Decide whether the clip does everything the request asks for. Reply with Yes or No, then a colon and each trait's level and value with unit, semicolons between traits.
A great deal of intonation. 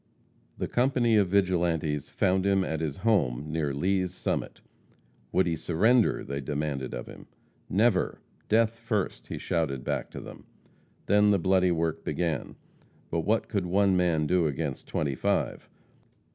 No: average, 4.6 semitones